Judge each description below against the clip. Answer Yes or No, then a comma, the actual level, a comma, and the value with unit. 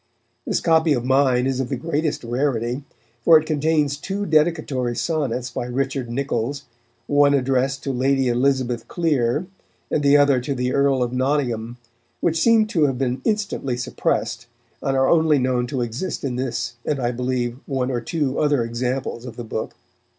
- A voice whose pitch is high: No, low, 135 Hz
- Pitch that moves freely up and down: No, average, 2.9 semitones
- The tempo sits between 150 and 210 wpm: Yes, average, 170 wpm